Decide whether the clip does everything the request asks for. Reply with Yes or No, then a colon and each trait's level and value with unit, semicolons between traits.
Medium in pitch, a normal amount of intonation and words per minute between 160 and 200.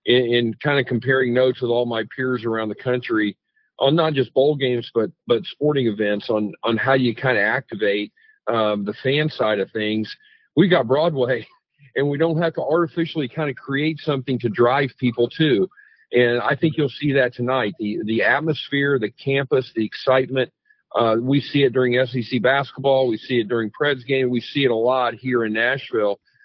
No: low, 130 Hz; average, 3.6 semitones; average, 195 wpm